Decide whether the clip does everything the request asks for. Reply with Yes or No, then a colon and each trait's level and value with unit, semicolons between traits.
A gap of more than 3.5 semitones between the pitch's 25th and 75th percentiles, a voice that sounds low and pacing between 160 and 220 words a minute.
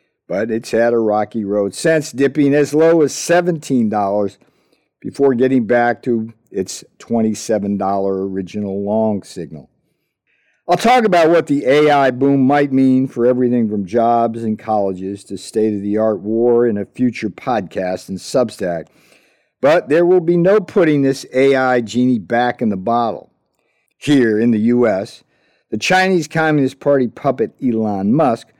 No: average, 4.7 semitones; low, 120 Hz; average, 150 wpm